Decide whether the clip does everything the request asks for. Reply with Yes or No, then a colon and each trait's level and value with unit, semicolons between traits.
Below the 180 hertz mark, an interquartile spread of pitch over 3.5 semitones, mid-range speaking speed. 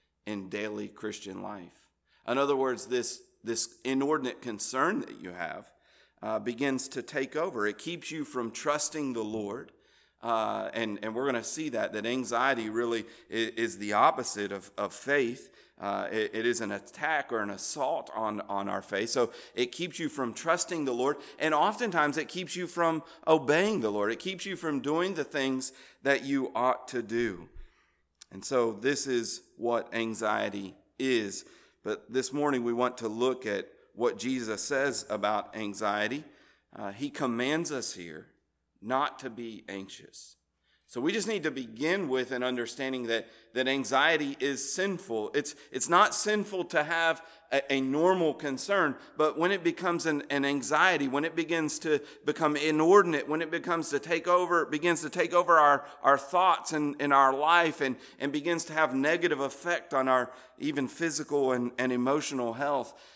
Yes: low, 135 Hz; average, 4.9 semitones; average, 175 wpm